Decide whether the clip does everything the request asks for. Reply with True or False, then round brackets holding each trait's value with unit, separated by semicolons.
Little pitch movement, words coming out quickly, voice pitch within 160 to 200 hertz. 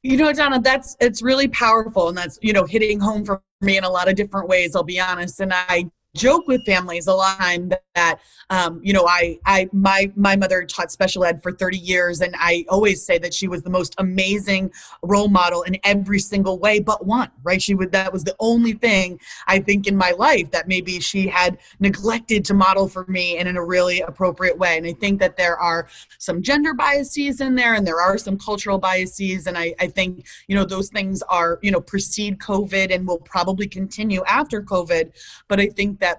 True (2.1 semitones; 220 wpm; 190 Hz)